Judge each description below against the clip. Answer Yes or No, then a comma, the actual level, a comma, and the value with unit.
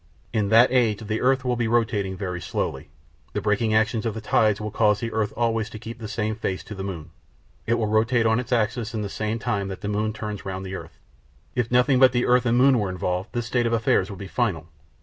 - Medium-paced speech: No, fast, 250 wpm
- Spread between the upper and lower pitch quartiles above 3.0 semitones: No, average, 2.7 semitones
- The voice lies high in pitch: No, low, 110 Hz